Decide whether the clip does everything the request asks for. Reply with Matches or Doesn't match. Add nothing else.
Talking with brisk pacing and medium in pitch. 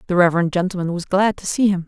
Matches